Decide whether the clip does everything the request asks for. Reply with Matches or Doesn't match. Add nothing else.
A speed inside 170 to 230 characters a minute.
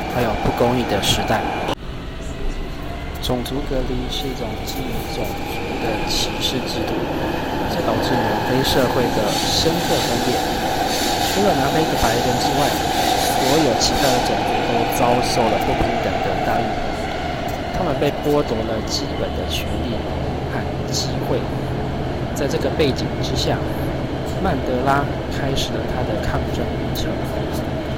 Matches